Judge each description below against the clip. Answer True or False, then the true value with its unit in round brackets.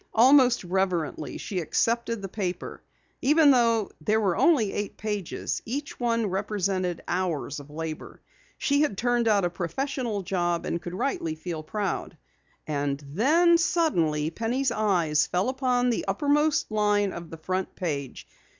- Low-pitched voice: False (205 Hz)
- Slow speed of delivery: False (145 wpm)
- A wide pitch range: True (5.9 semitones)